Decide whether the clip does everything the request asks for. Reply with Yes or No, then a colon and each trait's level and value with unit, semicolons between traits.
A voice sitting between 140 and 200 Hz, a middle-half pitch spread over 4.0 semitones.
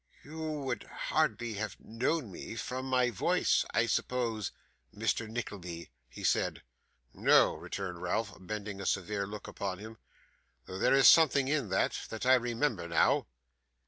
No: low, 110 Hz; average, 4.5 semitones